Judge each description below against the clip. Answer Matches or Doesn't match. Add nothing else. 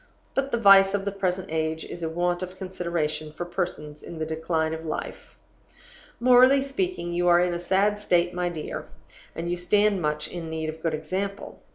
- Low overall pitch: Doesn't match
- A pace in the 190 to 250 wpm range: Matches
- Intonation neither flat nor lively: Matches